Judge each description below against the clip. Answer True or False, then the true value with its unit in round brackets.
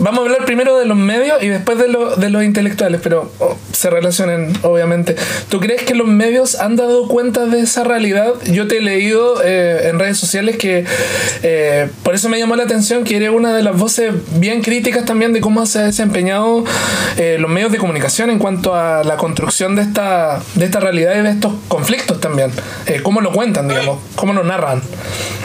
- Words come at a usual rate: False (205 wpm)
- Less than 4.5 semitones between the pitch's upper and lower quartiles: False (5.0 semitones)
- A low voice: False (205 Hz)